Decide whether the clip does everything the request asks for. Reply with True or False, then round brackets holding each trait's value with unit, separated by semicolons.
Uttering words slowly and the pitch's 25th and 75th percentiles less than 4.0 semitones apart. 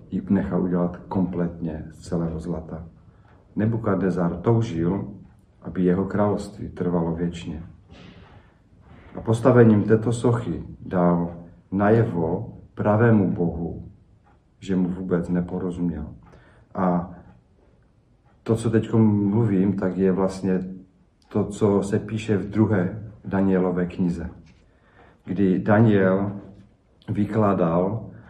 True (95 wpm; 2.8 semitones)